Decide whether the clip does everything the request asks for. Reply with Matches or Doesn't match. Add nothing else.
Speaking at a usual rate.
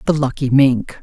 Matches